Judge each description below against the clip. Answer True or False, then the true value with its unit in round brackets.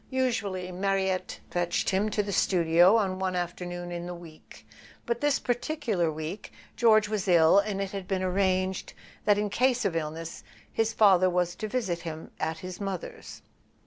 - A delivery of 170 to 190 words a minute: True (175 wpm)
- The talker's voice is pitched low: False (185 Hz)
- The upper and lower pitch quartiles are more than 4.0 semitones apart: False (2.9 semitones)